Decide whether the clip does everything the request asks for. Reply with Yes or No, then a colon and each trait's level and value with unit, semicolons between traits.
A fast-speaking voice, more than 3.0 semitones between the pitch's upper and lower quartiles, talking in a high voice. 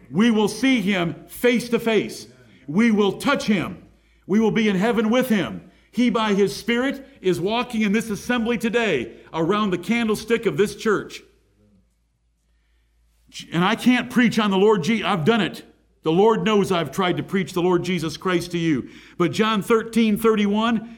No: average, 175 wpm; average, 4.4 semitones; high, 210 Hz